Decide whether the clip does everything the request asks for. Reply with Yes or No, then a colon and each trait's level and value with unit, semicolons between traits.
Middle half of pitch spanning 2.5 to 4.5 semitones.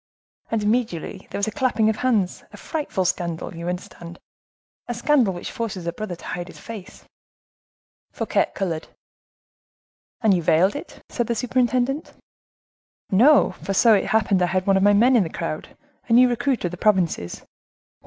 No: average, 5.1 semitones